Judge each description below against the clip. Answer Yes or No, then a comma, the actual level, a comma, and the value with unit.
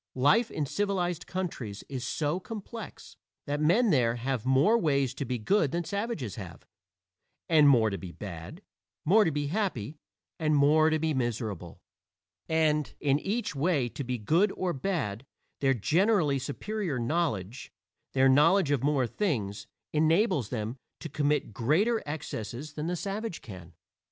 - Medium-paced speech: Yes, average, 150 wpm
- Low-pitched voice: No, medium, 145 Hz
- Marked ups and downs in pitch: Yes, wide, 6.1 semitones